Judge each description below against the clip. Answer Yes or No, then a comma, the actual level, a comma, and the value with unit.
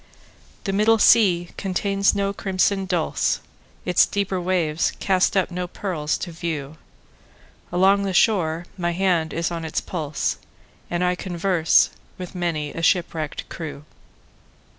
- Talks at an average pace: No, slow, 120 wpm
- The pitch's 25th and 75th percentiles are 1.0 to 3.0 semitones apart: Yes, average, 2.7 semitones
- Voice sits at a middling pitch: Yes, medium, 180 Hz